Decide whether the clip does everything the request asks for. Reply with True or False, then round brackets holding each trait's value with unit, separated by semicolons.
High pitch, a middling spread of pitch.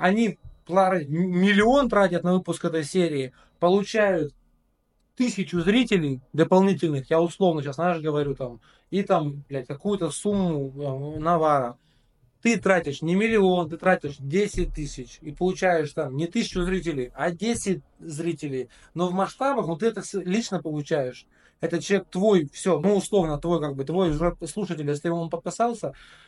False (175 Hz; 4.2 semitones)